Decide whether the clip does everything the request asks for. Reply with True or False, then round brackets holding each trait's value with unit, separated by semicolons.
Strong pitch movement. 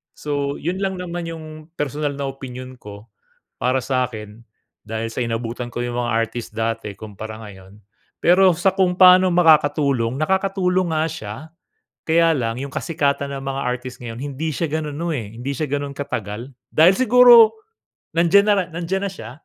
True (6.0 semitones)